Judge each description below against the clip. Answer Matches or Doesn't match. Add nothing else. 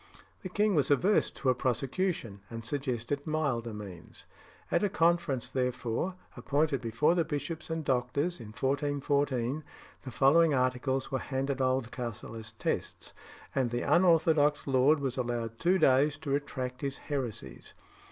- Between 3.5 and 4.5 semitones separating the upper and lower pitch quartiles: Matches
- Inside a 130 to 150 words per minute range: Matches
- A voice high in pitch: Doesn't match